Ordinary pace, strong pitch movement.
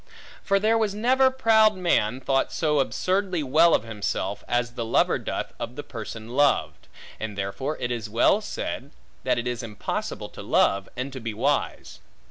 Yes: average, 175 wpm; wide, 8.4 semitones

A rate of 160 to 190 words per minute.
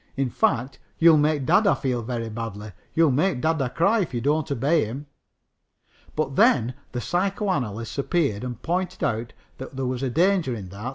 Yes: average, 170 wpm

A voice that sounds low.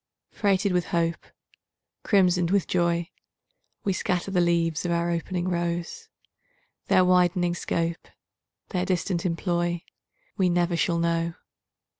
No: medium, 175 Hz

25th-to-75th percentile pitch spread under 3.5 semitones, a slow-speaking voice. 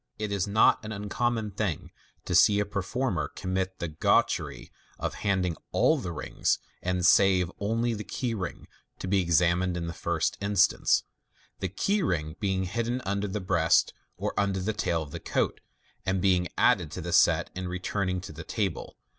No: average, 2.7 semitones; average, 175 wpm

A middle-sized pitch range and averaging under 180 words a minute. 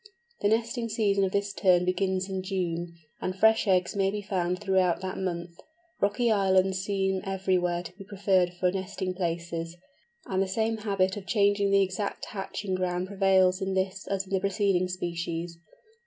No: narrow, 1.6 semitones; average, 170 wpm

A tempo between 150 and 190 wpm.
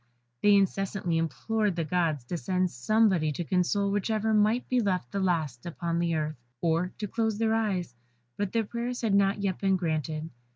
Yes: average, 175 wpm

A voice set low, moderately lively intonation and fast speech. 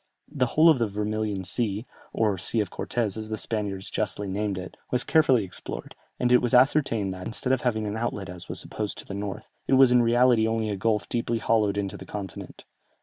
Yes: low, 110 Hz; average, 3.3 semitones; fast, 215 wpm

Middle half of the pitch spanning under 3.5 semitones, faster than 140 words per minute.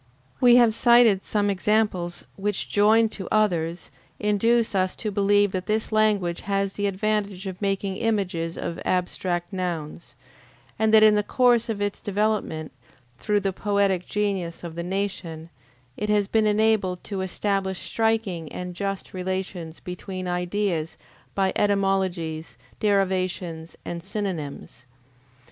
No: average, 2.8 semitones; slow, 135 wpm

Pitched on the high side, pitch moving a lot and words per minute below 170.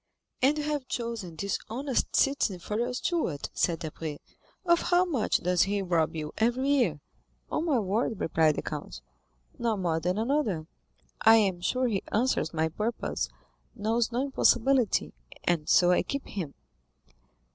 Yes: high, 220 Hz; wide, 6.8 semitones; average, 155 wpm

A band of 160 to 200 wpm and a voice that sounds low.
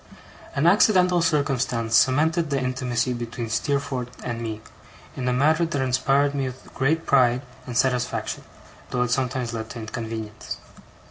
No: average, 145 wpm; low, 130 Hz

